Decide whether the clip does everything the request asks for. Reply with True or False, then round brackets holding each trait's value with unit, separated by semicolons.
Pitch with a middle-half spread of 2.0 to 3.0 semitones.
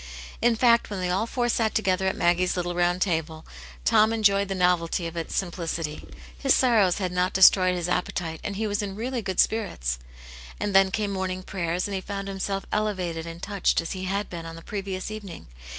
True (2.7 semitones)